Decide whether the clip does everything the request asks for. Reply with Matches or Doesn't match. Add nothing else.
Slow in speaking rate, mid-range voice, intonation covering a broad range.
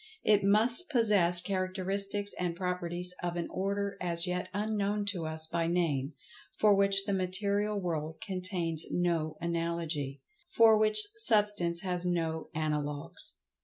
Doesn't match